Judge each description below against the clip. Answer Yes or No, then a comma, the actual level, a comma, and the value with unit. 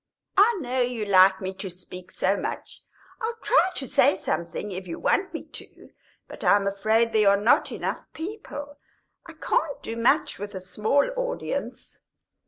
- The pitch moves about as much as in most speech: No, wide, 6.9 semitones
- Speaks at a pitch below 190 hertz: No, high, 220 Hz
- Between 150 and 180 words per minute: Yes, average, 170 wpm